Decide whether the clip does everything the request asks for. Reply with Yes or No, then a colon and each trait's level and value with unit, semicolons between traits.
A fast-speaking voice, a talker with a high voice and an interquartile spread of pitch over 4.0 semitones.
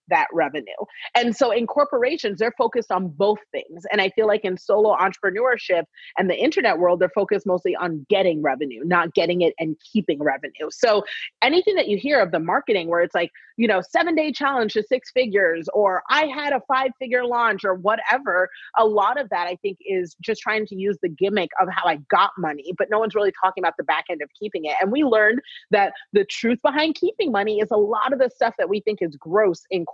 Yes: fast, 225 wpm; high, 210 Hz; average, 4.9 semitones